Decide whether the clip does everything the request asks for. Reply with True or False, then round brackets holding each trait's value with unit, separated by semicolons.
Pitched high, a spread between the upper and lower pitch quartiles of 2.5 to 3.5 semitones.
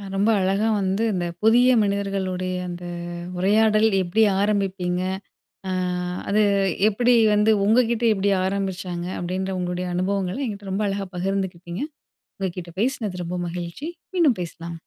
True (195 Hz; 2.8 semitones)